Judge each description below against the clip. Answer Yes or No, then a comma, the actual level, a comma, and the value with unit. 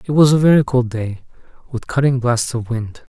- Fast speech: Yes, fast, 210 wpm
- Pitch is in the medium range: No, low, 125 Hz